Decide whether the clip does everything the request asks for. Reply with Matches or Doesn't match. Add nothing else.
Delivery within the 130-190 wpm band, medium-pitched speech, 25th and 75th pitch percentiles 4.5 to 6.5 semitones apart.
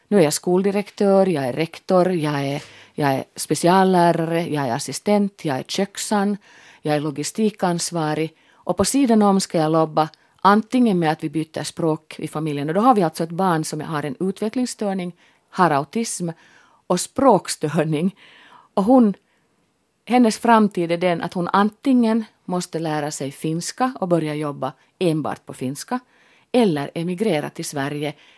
Matches